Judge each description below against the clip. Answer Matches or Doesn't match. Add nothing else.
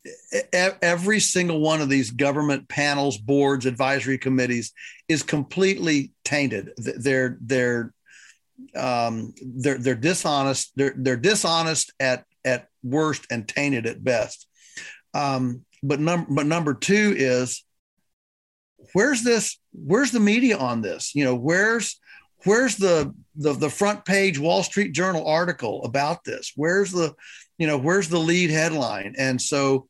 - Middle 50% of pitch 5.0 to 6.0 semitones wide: Matches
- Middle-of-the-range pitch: Matches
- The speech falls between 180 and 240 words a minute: Doesn't match